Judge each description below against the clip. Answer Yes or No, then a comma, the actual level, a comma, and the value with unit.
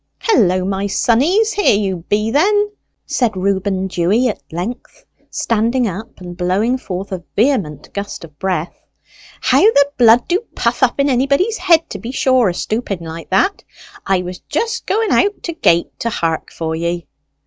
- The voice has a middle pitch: No, high, 215 Hz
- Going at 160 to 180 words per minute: Yes, average, 170 wpm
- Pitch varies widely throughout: Yes, wide, 6.9 semitones